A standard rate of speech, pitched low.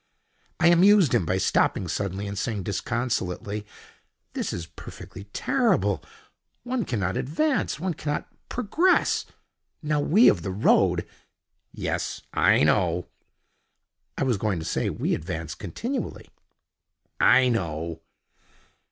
No: slow, 115 wpm; low, 105 Hz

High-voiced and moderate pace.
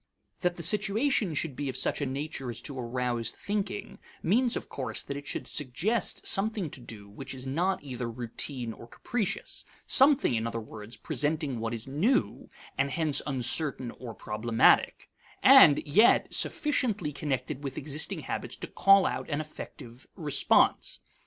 No: medium, 140 Hz; average, 160 wpm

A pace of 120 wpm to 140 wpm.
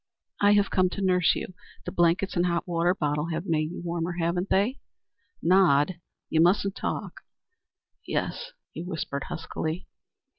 No: average, 150 wpm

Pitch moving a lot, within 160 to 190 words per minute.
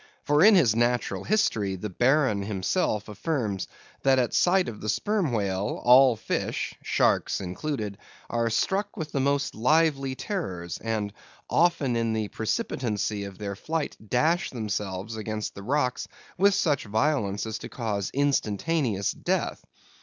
No: wide, 6.1 semitones; average, 145 wpm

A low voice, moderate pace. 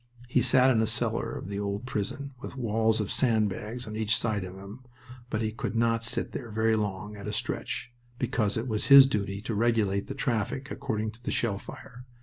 No: low, 110 Hz; fast, 210 wpm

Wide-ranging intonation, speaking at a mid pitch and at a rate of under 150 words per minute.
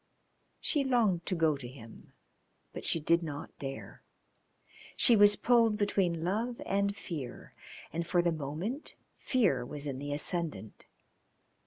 Yes: wide, 6.1 semitones; medium, 170 Hz; average, 140 wpm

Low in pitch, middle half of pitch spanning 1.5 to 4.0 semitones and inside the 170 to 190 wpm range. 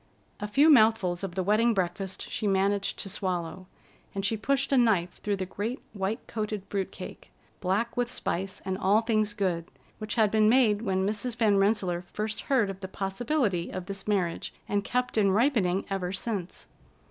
No: high, 205 Hz; average, 2.7 semitones; average, 180 wpm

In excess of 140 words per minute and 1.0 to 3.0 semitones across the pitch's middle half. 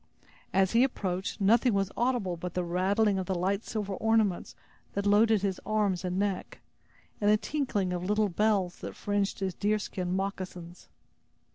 Yes: average, 165 wpm; narrow, 2.5 semitones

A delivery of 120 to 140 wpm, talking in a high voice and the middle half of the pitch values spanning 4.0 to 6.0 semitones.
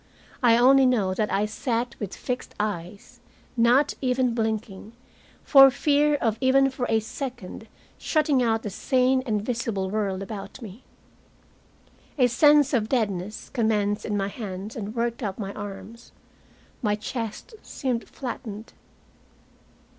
No: slow, 135 wpm; high, 230 Hz; average, 3.6 semitones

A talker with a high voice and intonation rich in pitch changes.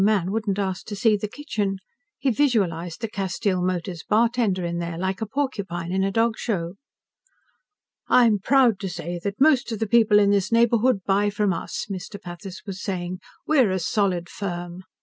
No: high, 200 Hz; average, 3.4 semitones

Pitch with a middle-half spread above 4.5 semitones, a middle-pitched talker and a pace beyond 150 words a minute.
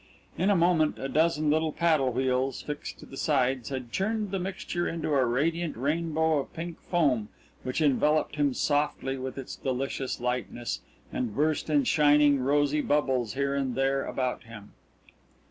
No: average, 3.5 semitones; medium, 145 Hz; average, 165 wpm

